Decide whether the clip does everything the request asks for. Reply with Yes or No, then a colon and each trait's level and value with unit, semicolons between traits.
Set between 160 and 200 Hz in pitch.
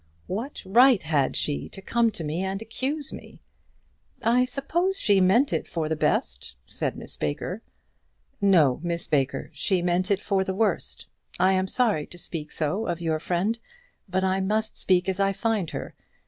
Yes: high, 190 Hz